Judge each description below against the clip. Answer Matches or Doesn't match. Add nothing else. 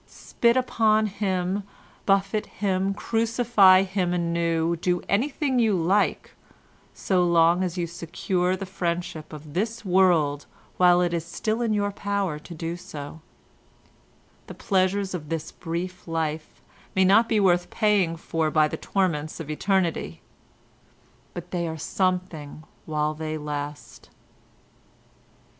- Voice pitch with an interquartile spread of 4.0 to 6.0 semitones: Doesn't match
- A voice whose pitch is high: Doesn't match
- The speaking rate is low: Matches